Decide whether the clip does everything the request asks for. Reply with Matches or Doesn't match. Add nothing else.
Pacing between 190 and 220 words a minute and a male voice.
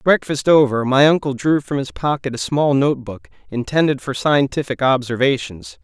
Doesn't match